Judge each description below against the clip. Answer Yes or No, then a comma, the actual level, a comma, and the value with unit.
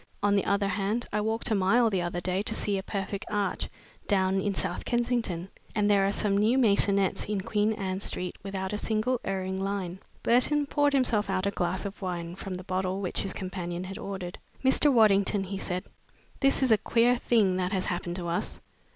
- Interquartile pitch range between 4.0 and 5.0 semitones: No, narrow, 2.6 semitones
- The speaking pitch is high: Yes, high, 195 Hz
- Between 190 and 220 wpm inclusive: Yes, fast, 205 wpm